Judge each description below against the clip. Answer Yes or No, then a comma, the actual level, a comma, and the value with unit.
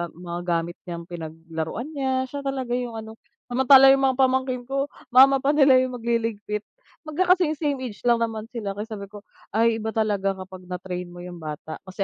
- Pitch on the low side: No, high, 230 Hz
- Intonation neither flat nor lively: No, wide, 5.9 semitones